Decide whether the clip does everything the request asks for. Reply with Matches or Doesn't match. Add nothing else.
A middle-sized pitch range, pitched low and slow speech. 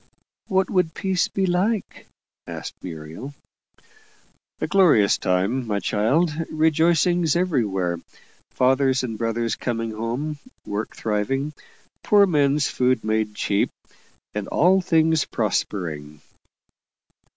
Doesn't match